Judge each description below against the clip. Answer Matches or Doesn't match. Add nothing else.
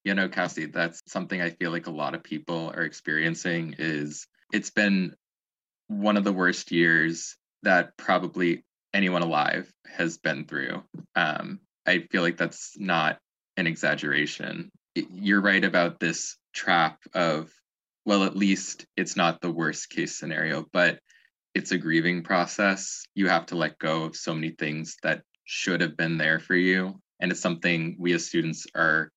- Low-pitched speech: Matches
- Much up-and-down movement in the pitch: Doesn't match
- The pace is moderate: Matches